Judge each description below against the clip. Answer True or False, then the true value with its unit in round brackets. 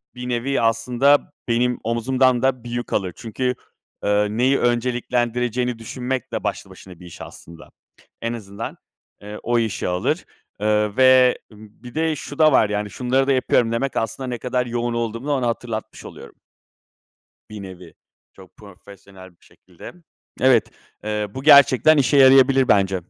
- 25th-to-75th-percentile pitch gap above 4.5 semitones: False (3.4 semitones)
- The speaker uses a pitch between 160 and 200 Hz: False (120 Hz)